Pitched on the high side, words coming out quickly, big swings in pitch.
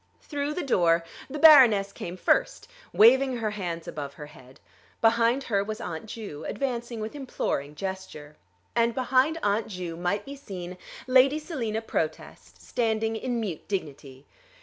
No: high, 220 Hz; average, 150 wpm; wide, 6.5 semitones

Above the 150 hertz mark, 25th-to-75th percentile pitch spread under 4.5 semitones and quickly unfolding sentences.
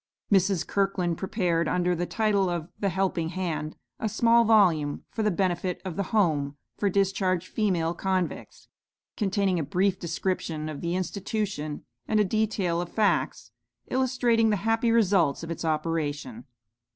No: medium, 185 Hz; average, 3.7 semitones; average, 150 wpm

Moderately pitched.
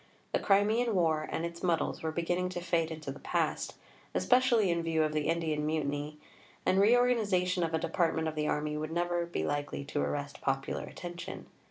Yes: medium, 165 Hz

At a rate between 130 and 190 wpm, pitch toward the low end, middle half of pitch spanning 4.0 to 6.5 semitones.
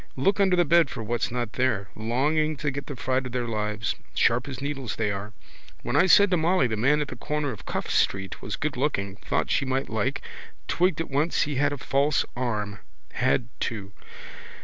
No: fast, 205 wpm; low, 130 Hz; average, 5.1 semitones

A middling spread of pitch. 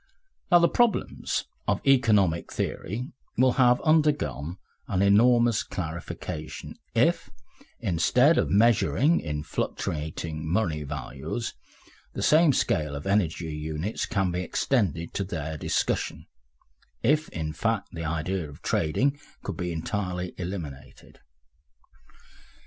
No: wide, 7.2 semitones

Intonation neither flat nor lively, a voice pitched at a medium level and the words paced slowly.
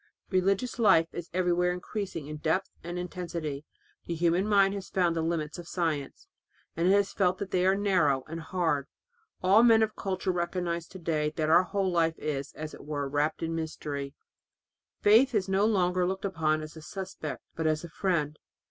No: average, 3.4 semitones; medium, 175 Hz; average, 190 wpm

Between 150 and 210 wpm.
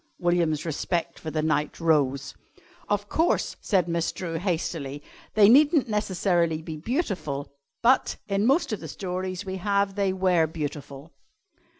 No: average, 140 wpm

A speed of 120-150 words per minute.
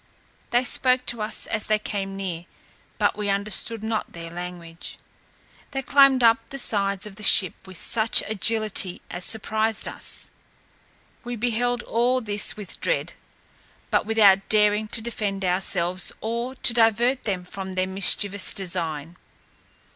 Yes: average, 145 wpm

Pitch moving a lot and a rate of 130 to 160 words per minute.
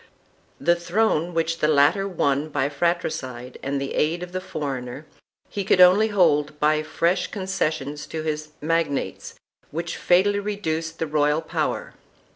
No: average, 3.3 semitones; average, 145 wpm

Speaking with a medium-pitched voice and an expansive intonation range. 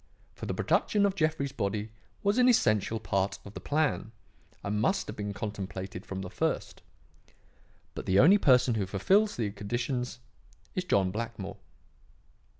No: low, 110 Hz; wide, 7.7 semitones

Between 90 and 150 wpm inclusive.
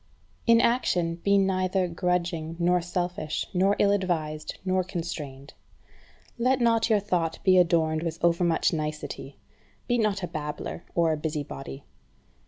Yes: average, 140 wpm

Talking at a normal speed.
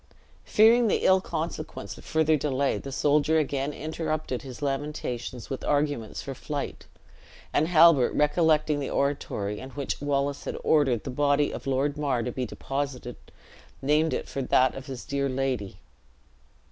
Yes: average, 155 wpm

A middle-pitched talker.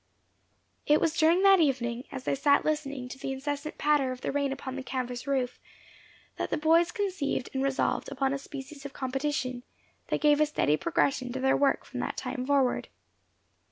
No: very high, 275 Hz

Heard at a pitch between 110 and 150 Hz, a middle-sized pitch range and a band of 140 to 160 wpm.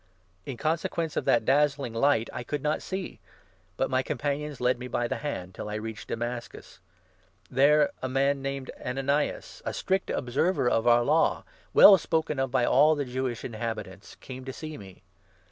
No: low, 135 Hz; average, 3.6 semitones; average, 180 wpm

